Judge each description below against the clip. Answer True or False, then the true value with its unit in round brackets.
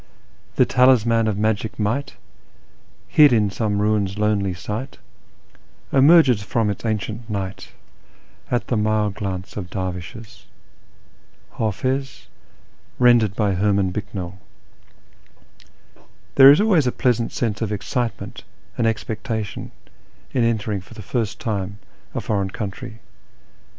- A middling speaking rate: False (125 wpm)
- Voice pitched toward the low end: True (110 Hz)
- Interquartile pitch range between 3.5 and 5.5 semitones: False (3.1 semitones)